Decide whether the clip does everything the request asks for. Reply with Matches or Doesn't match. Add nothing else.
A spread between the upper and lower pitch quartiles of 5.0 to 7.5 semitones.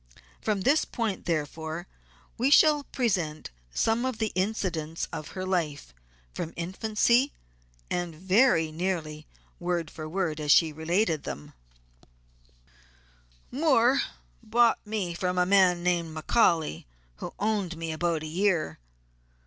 Matches